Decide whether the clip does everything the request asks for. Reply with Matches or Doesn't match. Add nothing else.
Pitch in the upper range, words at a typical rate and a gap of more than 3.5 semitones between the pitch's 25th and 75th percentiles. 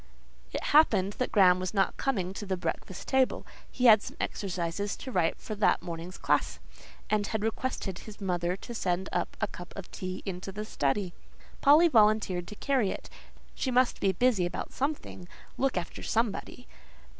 Matches